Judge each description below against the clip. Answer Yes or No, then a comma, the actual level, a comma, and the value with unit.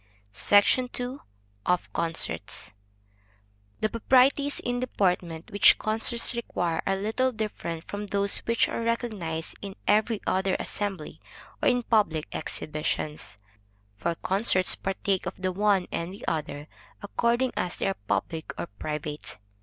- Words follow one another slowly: Yes, slow, 130 wpm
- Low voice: No, high, 195 Hz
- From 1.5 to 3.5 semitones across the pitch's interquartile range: No, wide, 5.6 semitones